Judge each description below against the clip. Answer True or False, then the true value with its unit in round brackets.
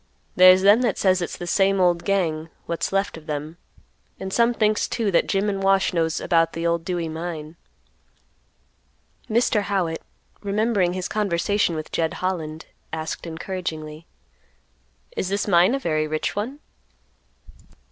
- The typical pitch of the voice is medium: True (180 Hz)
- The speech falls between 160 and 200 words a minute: False (145 wpm)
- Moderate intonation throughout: True (3.4 semitones)